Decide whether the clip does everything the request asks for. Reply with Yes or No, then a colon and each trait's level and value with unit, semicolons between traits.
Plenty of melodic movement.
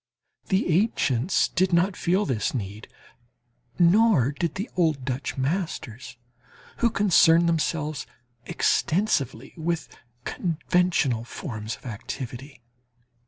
Yes: wide, 6.0 semitones